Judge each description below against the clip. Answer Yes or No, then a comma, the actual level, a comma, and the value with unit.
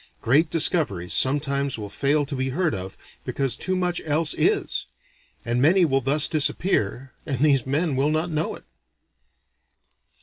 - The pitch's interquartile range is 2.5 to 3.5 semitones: Yes, average, 3.2 semitones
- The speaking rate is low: No, average, 155 wpm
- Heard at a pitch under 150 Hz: Yes, medium, 140 Hz